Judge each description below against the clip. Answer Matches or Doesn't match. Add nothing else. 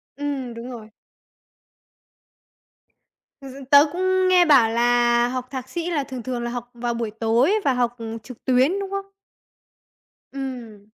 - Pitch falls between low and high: Doesn't match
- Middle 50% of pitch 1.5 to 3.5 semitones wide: Matches